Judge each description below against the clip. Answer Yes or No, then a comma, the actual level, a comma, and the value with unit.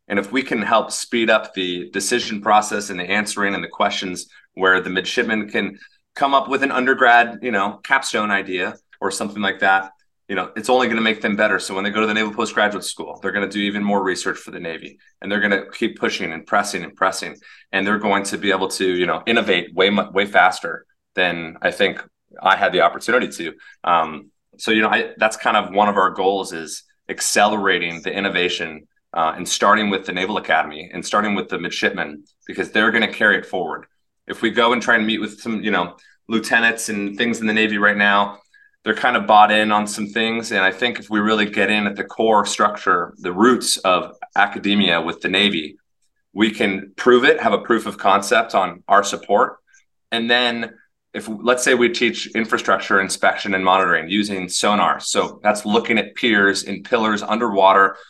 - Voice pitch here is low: Yes, low, 105 Hz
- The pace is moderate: No, fast, 215 wpm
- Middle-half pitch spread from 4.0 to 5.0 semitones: No, average, 2.8 semitones